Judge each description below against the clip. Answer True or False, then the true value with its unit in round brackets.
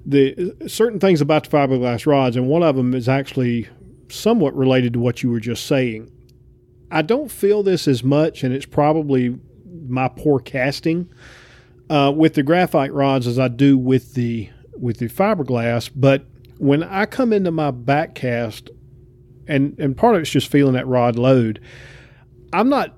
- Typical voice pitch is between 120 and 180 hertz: True (135 Hz)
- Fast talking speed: False (170 wpm)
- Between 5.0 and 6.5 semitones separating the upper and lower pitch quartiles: False (3.8 semitones)